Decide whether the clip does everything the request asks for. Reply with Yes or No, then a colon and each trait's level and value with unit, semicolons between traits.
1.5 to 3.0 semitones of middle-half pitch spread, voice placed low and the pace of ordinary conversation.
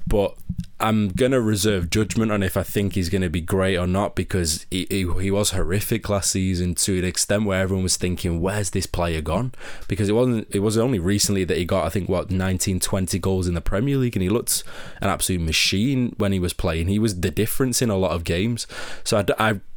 No: narrow, 2.6 semitones; very low, 95 Hz; fast, 230 wpm